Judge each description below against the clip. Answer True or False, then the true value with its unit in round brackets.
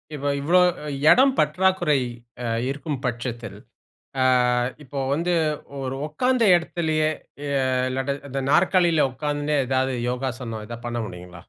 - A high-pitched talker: False (140 Hz)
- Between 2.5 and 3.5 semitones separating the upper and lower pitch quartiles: False (4.4 semitones)